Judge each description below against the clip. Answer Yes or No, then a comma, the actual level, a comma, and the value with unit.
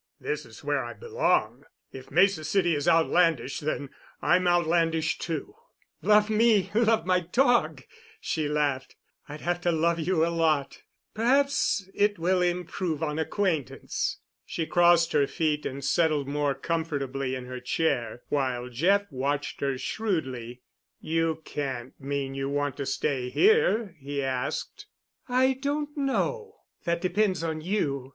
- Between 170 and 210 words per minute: No, average, 145 wpm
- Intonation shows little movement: No, average, 5.1 semitones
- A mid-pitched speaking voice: Yes, medium, 165 Hz